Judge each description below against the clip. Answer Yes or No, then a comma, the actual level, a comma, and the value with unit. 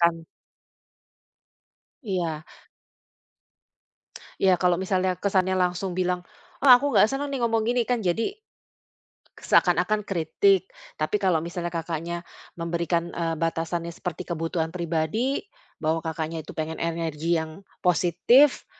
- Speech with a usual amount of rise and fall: Yes, average, 3.0 semitones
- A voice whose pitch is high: No, medium, 175 Hz